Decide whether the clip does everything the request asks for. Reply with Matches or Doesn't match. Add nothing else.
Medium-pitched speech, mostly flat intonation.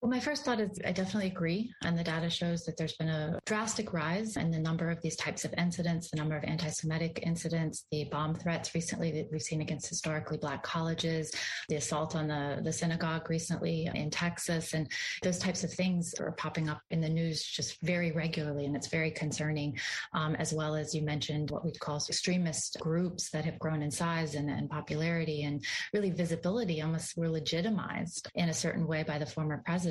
Matches